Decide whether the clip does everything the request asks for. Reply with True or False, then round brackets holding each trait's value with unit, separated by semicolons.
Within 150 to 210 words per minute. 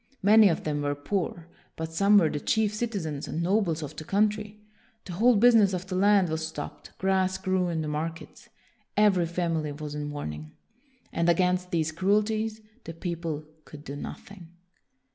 True (175 wpm)